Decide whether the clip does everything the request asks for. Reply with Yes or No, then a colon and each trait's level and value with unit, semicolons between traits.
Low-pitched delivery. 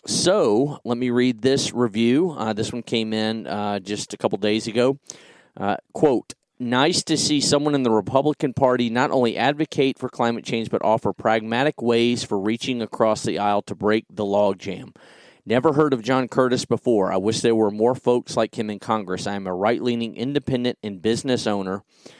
Yes: low, 115 Hz